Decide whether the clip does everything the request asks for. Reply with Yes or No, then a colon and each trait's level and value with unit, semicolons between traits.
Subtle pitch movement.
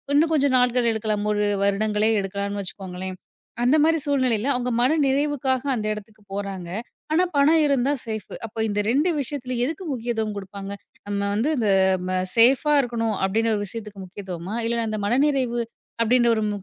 No: average, 4.3 semitones